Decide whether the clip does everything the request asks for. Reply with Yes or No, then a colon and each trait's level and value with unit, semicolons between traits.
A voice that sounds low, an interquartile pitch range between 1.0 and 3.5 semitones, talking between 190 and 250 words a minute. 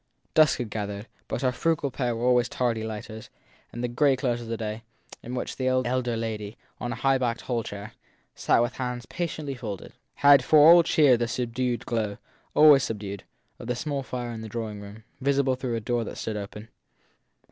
Yes: low, 120 Hz; narrow, 2.6 semitones; average, 195 wpm